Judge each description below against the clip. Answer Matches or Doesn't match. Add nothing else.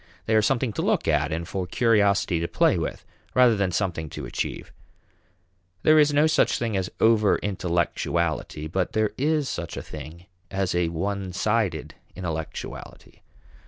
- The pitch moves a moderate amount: Matches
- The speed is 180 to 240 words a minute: Doesn't match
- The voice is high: Doesn't match